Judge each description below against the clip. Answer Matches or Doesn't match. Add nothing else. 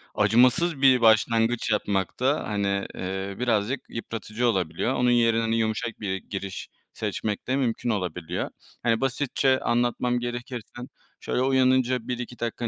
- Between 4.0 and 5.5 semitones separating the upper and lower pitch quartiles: Doesn't match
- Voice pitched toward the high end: Doesn't match